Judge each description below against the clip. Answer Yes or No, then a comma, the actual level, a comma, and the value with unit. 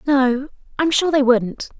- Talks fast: No, average, 165 wpm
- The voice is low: No, very high, 270 Hz